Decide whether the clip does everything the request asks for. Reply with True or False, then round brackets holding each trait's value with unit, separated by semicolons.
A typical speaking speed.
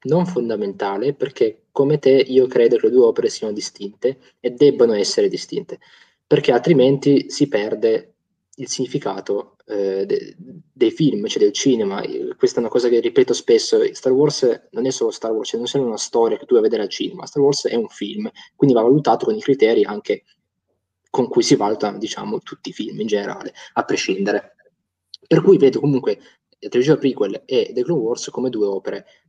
False (195 wpm)